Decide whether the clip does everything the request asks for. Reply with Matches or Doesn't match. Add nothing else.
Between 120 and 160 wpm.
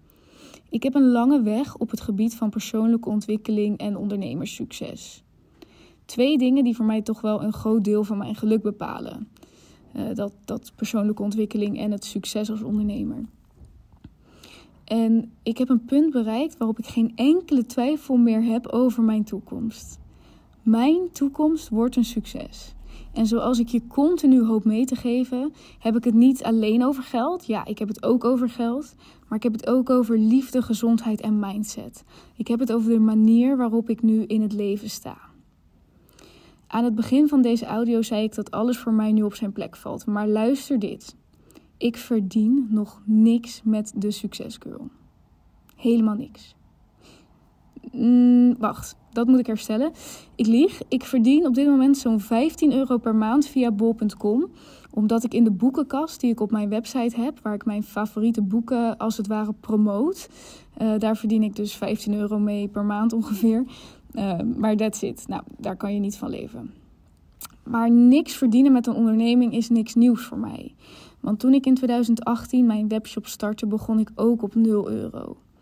Doesn't match